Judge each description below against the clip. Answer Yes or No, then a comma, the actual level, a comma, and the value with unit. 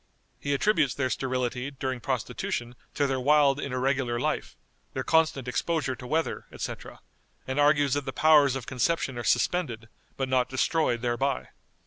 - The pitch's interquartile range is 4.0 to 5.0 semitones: No, narrow, 2.4 semitones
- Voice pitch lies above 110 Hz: Yes, low, 135 Hz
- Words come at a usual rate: Yes, average, 155 wpm